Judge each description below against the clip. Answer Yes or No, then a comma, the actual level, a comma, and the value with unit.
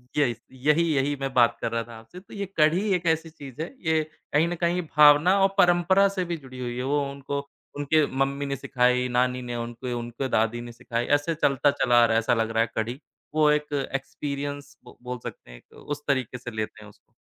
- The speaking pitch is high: No, low, 135 Hz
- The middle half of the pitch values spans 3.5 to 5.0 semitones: Yes, average, 4.0 semitones